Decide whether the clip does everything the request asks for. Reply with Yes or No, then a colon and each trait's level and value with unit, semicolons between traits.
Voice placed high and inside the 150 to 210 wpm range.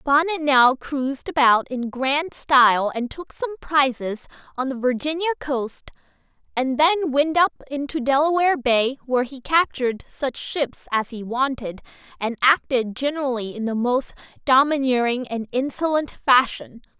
No: very high, 270 Hz; average, 140 wpm